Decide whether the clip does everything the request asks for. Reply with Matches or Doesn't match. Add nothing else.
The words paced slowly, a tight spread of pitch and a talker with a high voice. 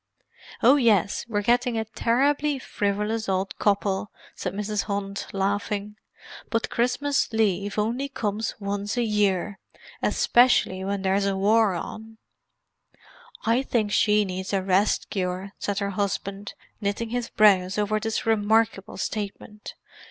Matches